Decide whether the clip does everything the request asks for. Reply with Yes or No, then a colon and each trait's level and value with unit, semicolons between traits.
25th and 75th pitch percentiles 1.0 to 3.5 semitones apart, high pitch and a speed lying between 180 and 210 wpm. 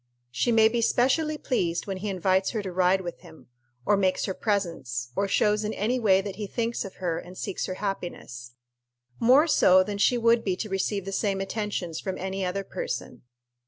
Yes: average, 2.8 semitones; high, 195 Hz; average, 200 wpm